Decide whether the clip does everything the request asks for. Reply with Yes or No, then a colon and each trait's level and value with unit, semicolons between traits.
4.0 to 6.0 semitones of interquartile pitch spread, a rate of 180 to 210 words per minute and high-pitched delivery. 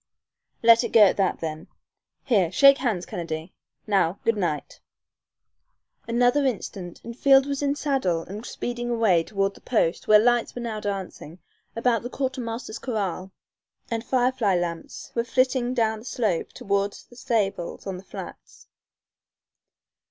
No: average, 4.3 semitones; average, 145 wpm; high, 225 Hz